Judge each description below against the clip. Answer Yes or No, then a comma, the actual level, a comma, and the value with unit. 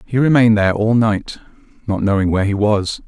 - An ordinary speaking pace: Yes, average, 195 wpm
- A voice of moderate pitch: No, low, 105 Hz